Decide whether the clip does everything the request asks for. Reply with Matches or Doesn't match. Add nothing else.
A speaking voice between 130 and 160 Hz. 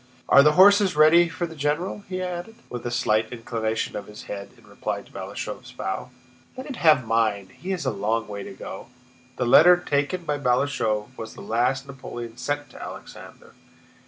Matches